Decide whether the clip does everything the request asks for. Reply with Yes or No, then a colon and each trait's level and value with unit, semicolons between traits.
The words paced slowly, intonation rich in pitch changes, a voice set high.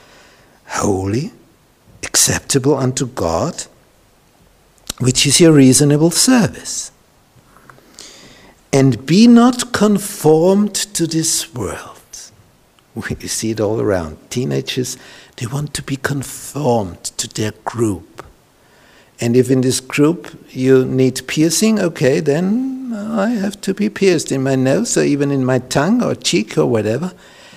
No: slow, 125 wpm; wide, 6.6 semitones; medium, 140 Hz